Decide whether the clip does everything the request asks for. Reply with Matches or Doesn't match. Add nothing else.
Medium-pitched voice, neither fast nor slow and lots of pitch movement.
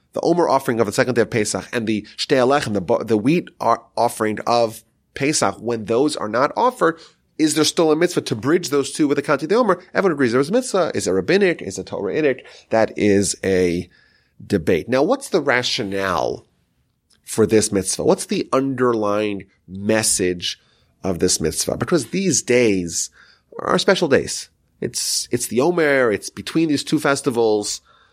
Doesn't match